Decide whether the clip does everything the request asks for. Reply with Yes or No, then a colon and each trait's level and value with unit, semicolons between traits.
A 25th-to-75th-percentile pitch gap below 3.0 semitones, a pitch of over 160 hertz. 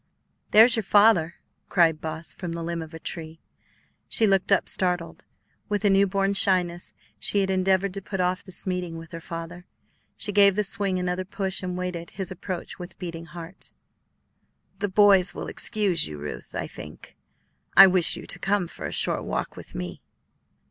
Yes: narrow, 2.5 semitones; medium, 185 Hz